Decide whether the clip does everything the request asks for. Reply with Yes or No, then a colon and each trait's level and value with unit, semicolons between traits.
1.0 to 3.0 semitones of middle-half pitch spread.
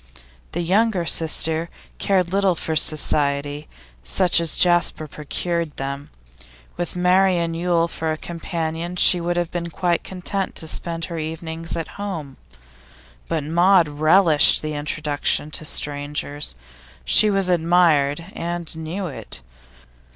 Yes: narrow, 2.4 semitones